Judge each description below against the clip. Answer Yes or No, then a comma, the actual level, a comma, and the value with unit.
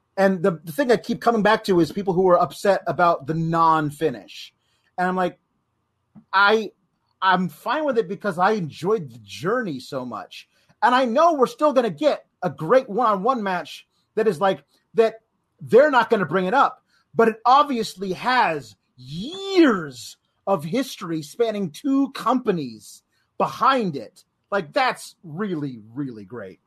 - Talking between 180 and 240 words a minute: No, average, 160 wpm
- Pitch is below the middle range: No, high, 195 Hz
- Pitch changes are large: Yes, wide, 6.2 semitones